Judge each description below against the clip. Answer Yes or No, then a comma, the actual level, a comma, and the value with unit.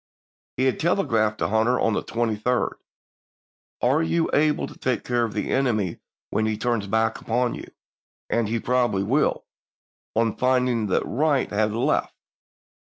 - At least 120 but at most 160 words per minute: Yes, average, 155 wpm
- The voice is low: Yes, low, 115 Hz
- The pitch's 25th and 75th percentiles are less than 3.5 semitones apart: Yes, average, 2.8 semitones